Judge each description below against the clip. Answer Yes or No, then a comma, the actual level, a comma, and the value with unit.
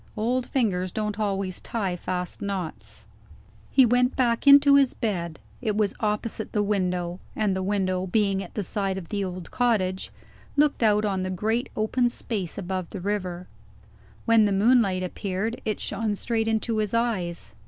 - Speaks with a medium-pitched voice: No, high, 205 Hz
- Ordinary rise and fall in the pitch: Yes, average, 3.5 semitones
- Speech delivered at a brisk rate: No, average, 165 wpm